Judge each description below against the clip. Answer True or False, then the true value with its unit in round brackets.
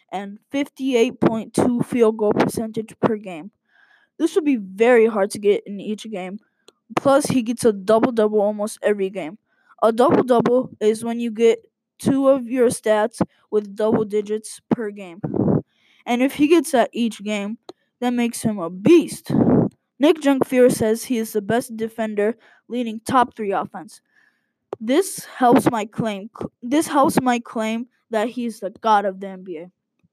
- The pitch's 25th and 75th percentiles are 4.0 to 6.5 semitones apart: False (2.8 semitones)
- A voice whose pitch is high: True (225 Hz)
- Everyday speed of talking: True (160 wpm)